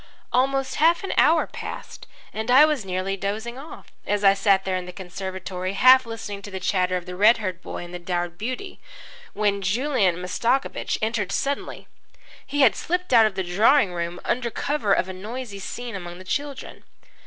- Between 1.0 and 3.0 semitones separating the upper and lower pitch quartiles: No, wide, 5.5 semitones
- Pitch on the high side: Yes, high, 205 Hz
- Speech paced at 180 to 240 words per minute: Yes, average, 190 wpm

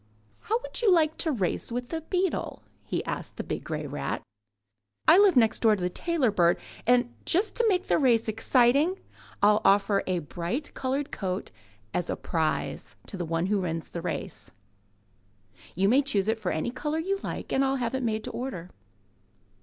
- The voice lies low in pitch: No, high, 235 Hz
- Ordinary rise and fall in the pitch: No, wide, 8.3 semitones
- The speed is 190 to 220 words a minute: Yes, average, 195 wpm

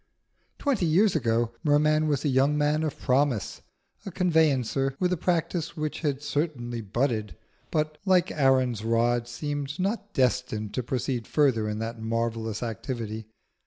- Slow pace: No, average, 145 wpm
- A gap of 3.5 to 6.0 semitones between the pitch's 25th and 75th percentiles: Yes, average, 4.8 semitones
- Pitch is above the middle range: No, low, 135 Hz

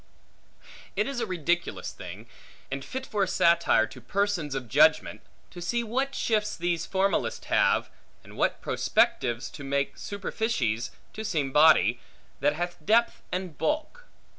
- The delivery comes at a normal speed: Yes, average, 145 wpm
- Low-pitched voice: No, medium, 175 Hz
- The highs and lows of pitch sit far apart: Yes, wide, 7.5 semitones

